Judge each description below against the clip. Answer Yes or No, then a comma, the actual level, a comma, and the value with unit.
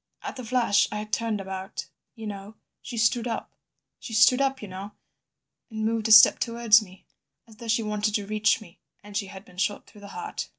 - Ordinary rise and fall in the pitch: No, narrow, 2.1 semitones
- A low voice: No, high, 215 Hz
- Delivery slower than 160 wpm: No, fast, 205 wpm